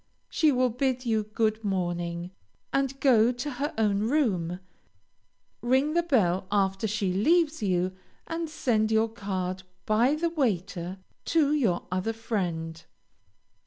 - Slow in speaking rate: Yes, slow, 130 wpm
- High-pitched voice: Yes, high, 220 Hz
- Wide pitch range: Yes, wide, 6.2 semitones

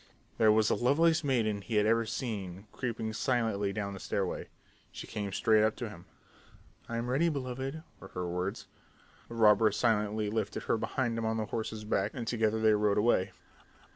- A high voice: No, low, 110 Hz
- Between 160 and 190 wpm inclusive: Yes, average, 180 wpm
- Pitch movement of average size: No, narrow, 2.3 semitones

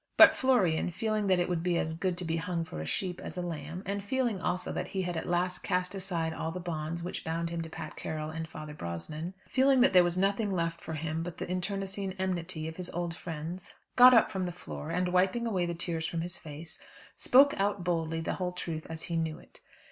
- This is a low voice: No, medium, 175 Hz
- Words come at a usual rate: No, fast, 240 wpm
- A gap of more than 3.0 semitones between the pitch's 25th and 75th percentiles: No, narrow, 2.6 semitones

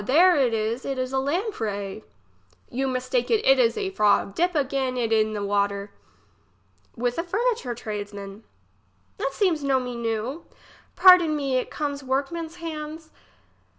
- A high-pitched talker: Yes, very high, 265 Hz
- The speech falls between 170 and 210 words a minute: No, average, 150 wpm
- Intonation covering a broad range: Yes, wide, 6.8 semitones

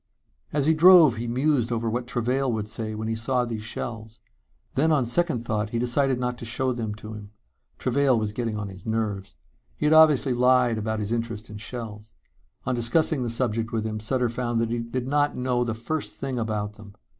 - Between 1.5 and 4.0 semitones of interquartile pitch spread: Yes, average, 2.7 semitones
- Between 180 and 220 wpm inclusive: Yes, fast, 205 wpm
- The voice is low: Yes, low, 120 Hz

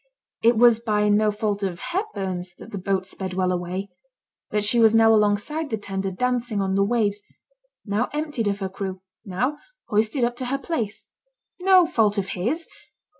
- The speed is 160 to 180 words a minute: Yes, average, 175 wpm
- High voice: Yes, high, 210 Hz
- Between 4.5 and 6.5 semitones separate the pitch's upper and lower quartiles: No, average, 3.8 semitones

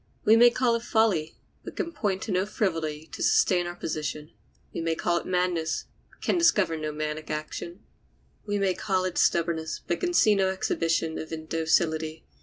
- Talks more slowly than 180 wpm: No, average, 185 wpm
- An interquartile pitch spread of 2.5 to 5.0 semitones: Yes, average, 4.0 semitones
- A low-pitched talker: No, medium, 175 Hz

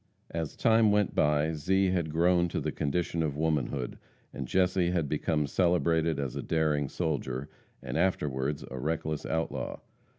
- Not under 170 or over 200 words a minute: No, average, 155 wpm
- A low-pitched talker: Yes, very low, 80 Hz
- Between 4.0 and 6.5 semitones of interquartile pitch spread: No, average, 3.3 semitones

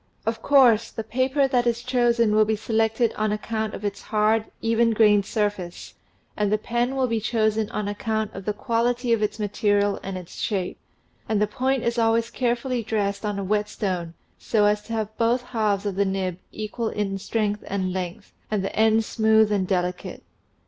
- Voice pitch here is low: No, high, 215 Hz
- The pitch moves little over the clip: Yes, narrow, 2.1 semitones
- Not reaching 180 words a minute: No, average, 190 wpm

